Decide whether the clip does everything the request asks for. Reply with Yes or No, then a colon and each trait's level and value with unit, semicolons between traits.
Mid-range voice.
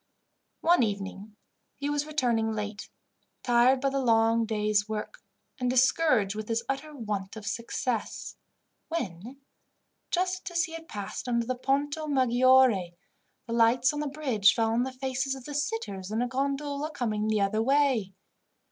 No: high, 245 Hz